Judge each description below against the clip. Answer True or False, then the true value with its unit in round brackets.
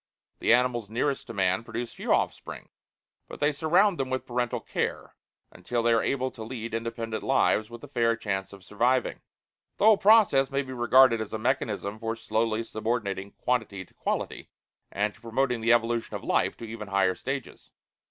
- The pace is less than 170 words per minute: False (180 wpm)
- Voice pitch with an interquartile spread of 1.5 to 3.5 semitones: True (2.9 semitones)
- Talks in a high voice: False (115 Hz)